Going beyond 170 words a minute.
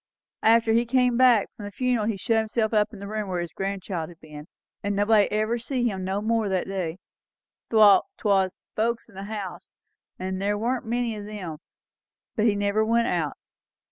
Yes: fast, 205 wpm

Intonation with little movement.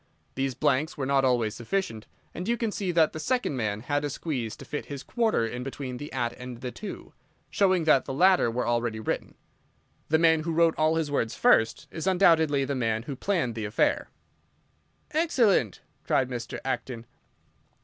No: wide, 5.5 semitones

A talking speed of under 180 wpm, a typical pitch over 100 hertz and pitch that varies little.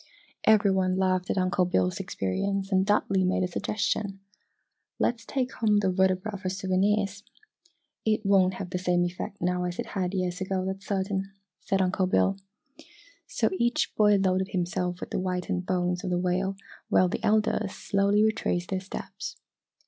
Yes: average, 165 wpm; high, 190 Hz; narrow, 1.7 semitones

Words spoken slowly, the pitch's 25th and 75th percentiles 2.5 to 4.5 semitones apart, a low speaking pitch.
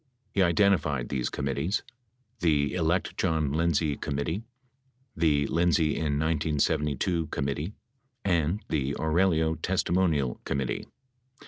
Yes: slow, 105 wpm; average, 3.1 semitones; very low, 80 Hz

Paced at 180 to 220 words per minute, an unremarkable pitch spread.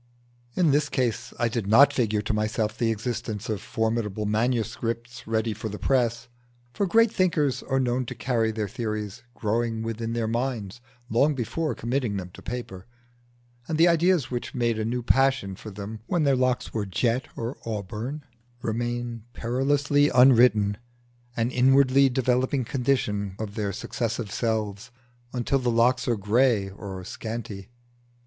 No: average, 155 wpm; average, 3.1 semitones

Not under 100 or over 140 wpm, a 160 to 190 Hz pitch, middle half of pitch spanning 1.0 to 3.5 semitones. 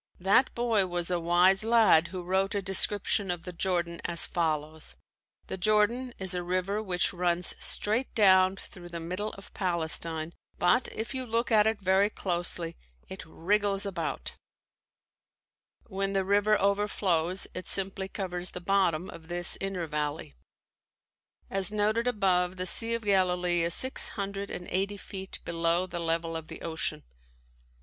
No: average, 155 wpm; medium, 185 Hz; average, 2.7 semitones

